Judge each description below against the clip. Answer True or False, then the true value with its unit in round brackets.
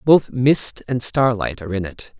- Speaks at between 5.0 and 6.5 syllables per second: False (4.4 syllables/s)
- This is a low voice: True (120 Hz)